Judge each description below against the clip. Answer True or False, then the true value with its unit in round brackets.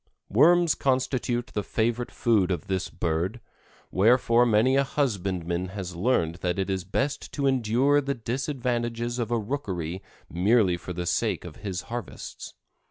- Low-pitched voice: True (115 Hz)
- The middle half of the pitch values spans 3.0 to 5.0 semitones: False (5.4 semitones)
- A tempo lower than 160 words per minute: True (150 wpm)